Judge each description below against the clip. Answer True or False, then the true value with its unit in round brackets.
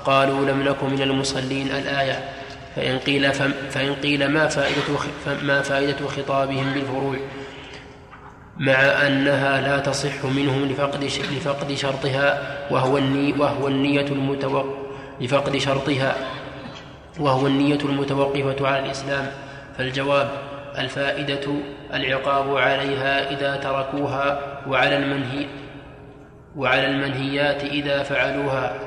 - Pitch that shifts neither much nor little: False (0.5 semitones)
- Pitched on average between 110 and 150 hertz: True (140 Hz)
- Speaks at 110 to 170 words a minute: False (85 wpm)